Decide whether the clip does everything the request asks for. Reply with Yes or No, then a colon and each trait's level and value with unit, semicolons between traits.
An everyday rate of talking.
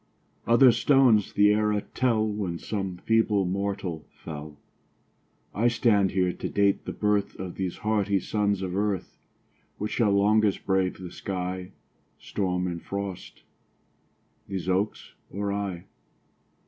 No: slow, 130 wpm